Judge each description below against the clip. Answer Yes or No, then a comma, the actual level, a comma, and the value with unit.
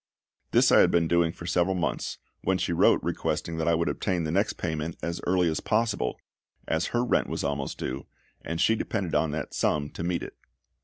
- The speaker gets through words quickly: Yes, fast, 210 wpm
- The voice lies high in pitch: No, very low, 85 Hz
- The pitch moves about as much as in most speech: No, narrow, 2.2 semitones